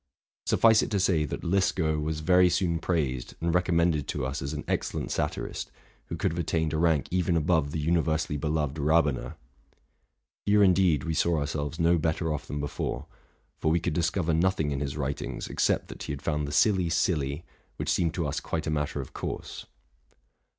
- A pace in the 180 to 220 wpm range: Yes, average, 190 wpm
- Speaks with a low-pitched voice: Yes, very low, 80 Hz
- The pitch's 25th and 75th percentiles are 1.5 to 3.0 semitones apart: Yes, average, 2.7 semitones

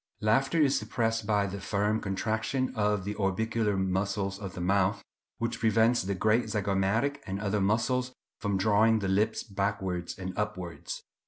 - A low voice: Yes, low, 105 Hz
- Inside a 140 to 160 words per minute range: Yes, average, 155 wpm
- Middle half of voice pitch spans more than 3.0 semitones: No, narrow, 2.5 semitones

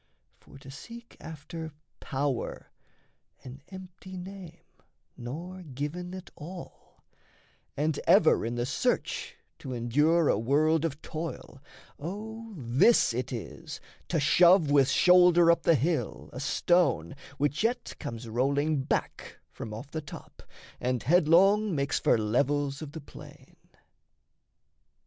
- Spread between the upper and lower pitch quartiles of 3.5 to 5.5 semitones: Yes, average, 4.8 semitones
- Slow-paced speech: Yes, slow, 125 wpm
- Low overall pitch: No, medium, 155 Hz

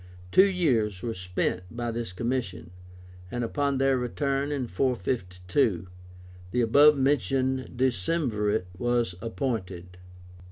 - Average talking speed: No, slow, 110 wpm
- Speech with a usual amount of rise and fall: No, wide, 6.2 semitones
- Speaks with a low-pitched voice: Yes, low, 120 Hz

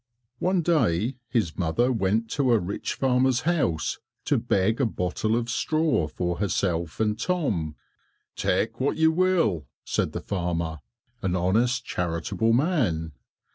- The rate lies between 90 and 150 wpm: Yes, slow, 135 wpm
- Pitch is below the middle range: Yes, low, 110 Hz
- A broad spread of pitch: Yes, wide, 7.1 semitones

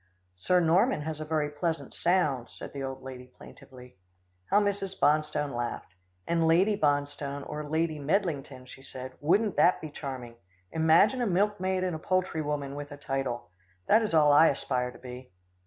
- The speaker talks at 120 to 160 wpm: No, average, 170 wpm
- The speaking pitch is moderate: Yes, medium, 150 Hz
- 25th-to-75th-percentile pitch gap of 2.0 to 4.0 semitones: No, average, 4.7 semitones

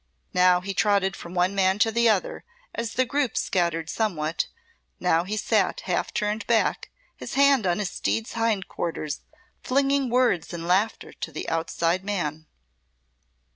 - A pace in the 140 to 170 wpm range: Yes, average, 155 wpm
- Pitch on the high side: Yes, high, 200 Hz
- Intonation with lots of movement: No, average, 4.8 semitones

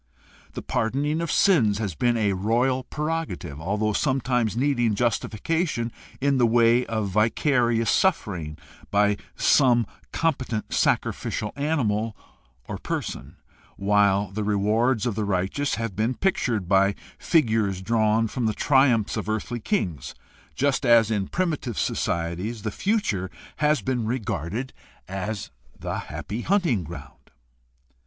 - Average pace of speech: No, slow, 130 wpm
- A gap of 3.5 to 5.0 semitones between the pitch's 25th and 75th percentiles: Yes, average, 4.3 semitones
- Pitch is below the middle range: Yes, low, 115 Hz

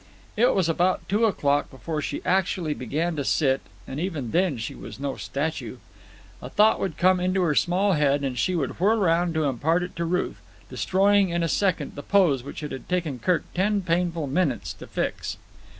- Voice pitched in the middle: Yes, medium, 170 Hz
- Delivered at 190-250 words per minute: Yes, average, 200 wpm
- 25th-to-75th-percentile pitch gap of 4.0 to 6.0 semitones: Yes, average, 4.3 semitones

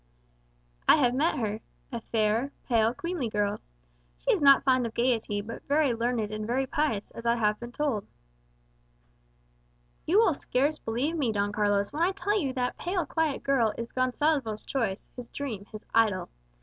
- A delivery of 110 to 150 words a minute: No, average, 175 wpm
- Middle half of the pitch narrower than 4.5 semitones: No, average, 4.8 semitones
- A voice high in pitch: Yes, high, 240 Hz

